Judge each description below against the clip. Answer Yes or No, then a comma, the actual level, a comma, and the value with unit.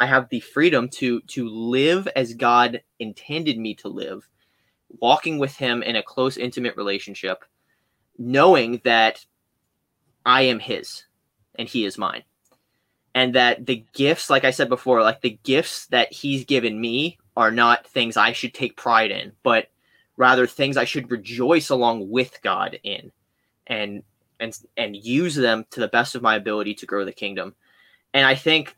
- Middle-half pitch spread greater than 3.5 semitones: No, average, 2.7 semitones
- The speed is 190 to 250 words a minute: No, average, 170 wpm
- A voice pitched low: Yes, low, 120 Hz